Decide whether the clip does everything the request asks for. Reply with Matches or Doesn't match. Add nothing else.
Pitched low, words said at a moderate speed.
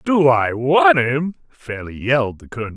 Matches